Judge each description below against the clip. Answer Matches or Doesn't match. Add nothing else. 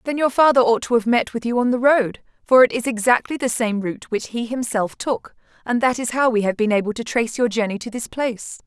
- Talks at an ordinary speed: Doesn't match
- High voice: Matches